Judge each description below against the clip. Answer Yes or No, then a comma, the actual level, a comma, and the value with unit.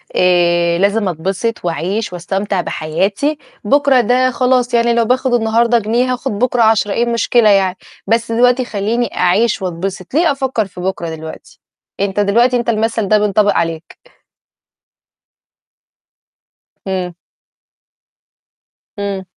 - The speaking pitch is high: Yes, high, 215 Hz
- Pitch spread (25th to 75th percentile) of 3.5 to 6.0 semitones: Yes, average, 4.1 semitones